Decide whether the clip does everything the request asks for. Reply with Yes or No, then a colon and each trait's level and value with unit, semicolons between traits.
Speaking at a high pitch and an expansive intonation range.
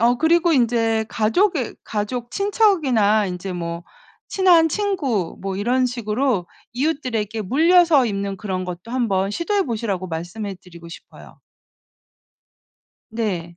Yes: high, 225 Hz; wide, 6.7 semitones